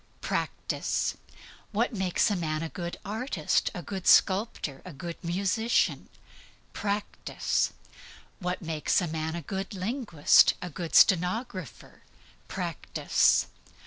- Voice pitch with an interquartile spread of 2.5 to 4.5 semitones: Yes, average, 3.6 semitones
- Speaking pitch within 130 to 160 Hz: No, medium, 180 Hz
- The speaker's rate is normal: No, slow, 115 wpm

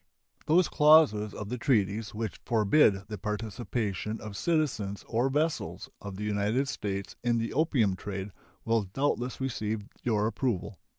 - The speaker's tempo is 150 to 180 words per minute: No, average, 140 wpm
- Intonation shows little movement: No, average, 4.1 semitones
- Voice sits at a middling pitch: No, low, 110 Hz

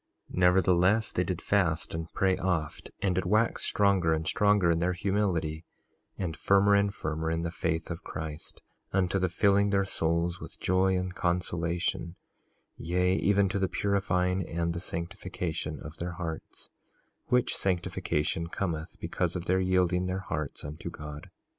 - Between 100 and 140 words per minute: No, average, 160 wpm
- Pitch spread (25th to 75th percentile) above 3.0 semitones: No, narrow, 2.5 semitones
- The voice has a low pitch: Yes, very low, 90 Hz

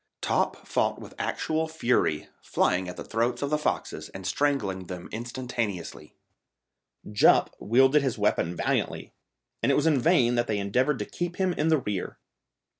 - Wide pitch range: Yes, wide, 6.7 semitones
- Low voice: Yes, low, 120 Hz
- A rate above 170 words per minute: No, average, 165 wpm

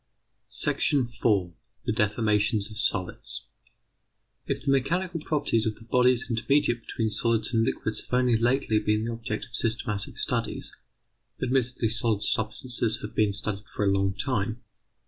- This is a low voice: Yes, low, 115 Hz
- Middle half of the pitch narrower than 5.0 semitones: Yes, narrow, 2.6 semitones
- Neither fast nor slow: Yes, average, 145 wpm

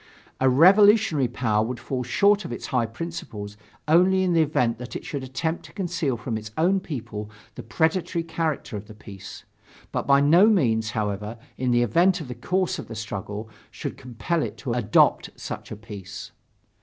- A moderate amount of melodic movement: No, wide, 7.1 semitones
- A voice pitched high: No, low, 130 Hz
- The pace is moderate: Yes, average, 185 wpm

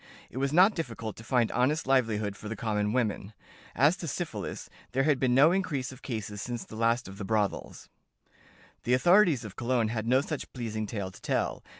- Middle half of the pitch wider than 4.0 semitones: No, average, 3.7 semitones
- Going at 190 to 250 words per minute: Yes, average, 200 wpm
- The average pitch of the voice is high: No, low, 120 Hz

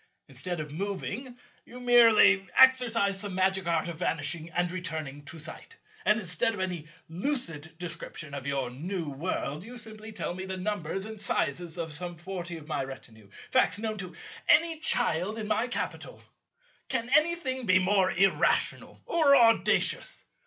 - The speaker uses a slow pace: No, average, 160 wpm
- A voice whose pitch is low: No, medium, 185 Hz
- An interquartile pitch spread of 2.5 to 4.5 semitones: No, average, 5.3 semitones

